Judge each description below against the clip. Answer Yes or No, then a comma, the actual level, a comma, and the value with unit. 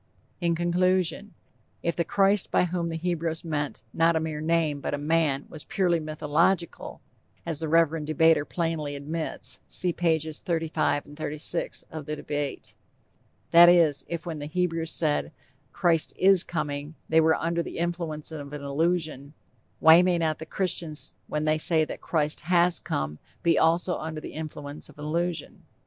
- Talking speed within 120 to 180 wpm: Yes, average, 165 wpm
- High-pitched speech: No, medium, 160 Hz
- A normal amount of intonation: No, narrow, 2.1 semitones